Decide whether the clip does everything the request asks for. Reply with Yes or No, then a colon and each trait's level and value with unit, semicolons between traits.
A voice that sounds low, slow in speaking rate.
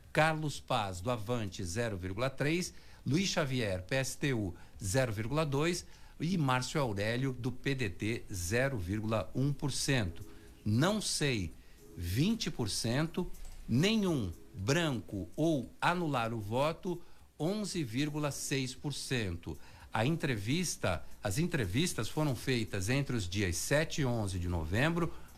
Yes: low, 130 Hz; slow, 90 wpm